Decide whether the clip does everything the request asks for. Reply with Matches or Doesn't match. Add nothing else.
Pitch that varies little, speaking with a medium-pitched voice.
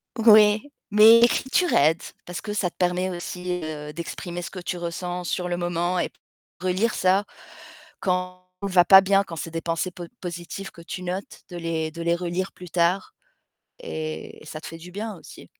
Matches